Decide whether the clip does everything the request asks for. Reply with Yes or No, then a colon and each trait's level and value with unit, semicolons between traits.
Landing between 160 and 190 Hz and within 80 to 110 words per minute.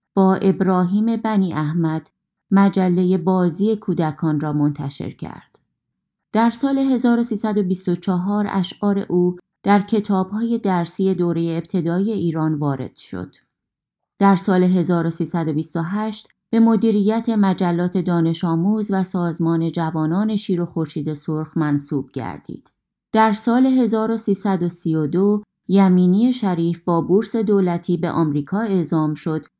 Yes: medium, 185 Hz; slow, 105 wpm